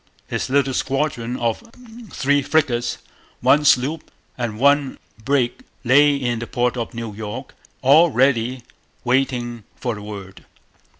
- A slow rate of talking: Yes, slow, 130 wpm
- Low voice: Yes, low, 125 Hz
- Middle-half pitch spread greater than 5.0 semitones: No, average, 3.1 semitones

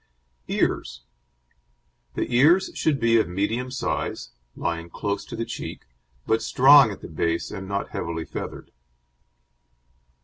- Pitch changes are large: Yes, wide, 6.7 semitones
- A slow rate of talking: Yes, slow, 130 wpm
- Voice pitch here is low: Yes, low, 110 Hz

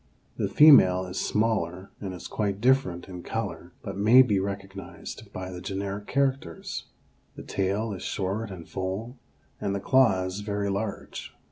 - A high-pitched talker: No, low, 100 Hz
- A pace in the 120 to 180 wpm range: Yes, average, 150 wpm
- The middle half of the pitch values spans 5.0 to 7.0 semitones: No, average, 3.0 semitones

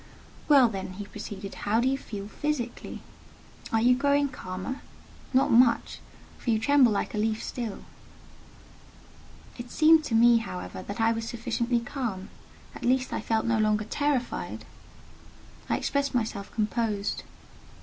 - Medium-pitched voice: No, high, 230 Hz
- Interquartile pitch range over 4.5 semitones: No, average, 3.3 semitones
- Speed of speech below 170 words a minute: Yes, average, 145 wpm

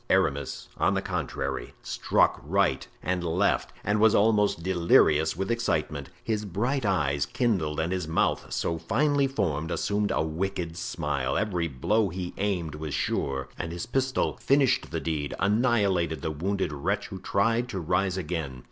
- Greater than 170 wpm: No, average, 155 wpm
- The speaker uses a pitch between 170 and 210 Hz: No, very low, 90 Hz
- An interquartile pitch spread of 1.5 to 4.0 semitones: No, average, 4.8 semitones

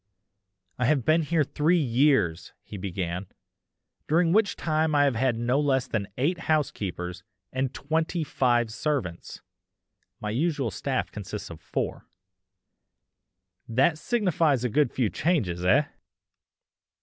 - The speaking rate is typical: No, slow, 125 wpm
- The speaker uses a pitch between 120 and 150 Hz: Yes, low, 135 Hz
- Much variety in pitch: Yes, wide, 5.7 semitones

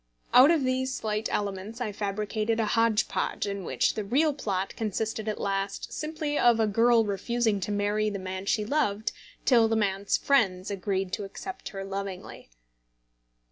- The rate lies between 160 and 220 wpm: Yes, average, 170 wpm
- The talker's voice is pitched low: No, high, 215 Hz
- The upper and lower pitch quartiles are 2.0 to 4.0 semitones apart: Yes, average, 3.1 semitones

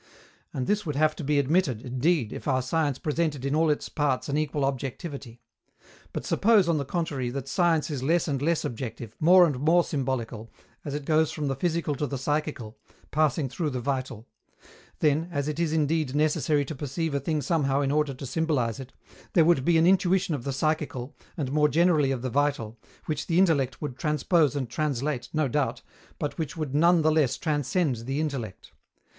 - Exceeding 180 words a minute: Yes, average, 195 wpm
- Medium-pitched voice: Yes, medium, 145 Hz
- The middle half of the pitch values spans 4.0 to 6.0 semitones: No, average, 3.1 semitones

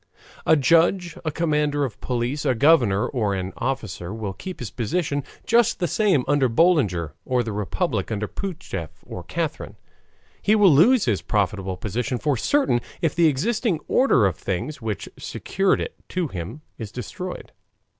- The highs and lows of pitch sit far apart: Yes, wide, 8.0 semitones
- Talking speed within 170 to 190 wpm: No, average, 160 wpm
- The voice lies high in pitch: No, low, 135 Hz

